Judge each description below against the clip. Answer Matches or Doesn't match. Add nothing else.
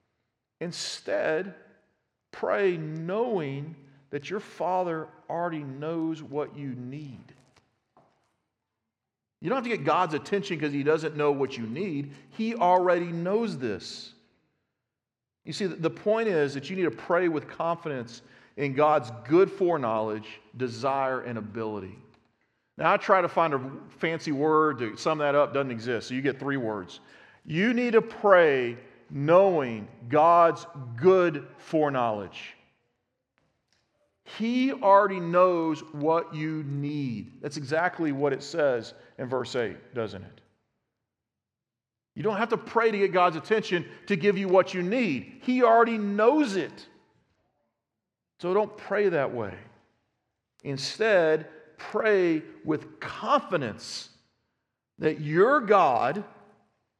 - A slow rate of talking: Matches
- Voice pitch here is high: Doesn't match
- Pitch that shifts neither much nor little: Doesn't match